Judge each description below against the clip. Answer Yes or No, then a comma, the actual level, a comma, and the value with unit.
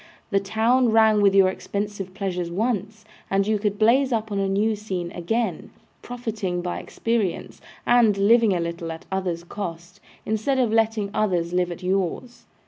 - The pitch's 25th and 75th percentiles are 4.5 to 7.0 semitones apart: No, average, 3.5 semitones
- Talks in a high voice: Yes, high, 200 Hz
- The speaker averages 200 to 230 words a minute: No, average, 165 wpm